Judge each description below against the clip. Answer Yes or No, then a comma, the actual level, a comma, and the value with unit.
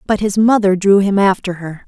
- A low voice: No, high, 195 Hz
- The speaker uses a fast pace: Yes, fast, 225 wpm